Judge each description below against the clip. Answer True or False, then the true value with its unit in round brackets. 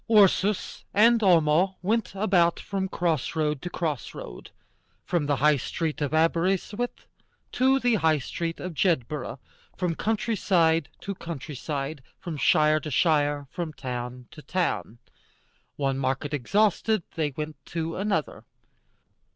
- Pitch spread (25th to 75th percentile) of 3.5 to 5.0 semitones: True (4.5 semitones)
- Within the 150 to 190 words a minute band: False (140 wpm)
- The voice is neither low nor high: True (165 Hz)